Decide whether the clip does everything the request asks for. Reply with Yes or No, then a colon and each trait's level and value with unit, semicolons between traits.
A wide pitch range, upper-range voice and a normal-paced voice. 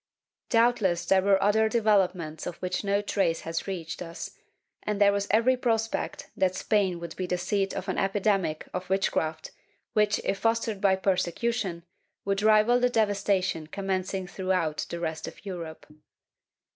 No: average, 2.9 semitones; high, 195 Hz; average, 160 wpm